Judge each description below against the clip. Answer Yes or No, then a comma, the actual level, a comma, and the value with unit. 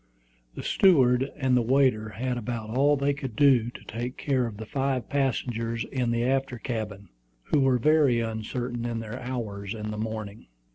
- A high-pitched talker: No, low, 120 Hz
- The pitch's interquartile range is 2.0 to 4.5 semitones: Yes, average, 3.1 semitones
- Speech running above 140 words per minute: Yes, average, 180 wpm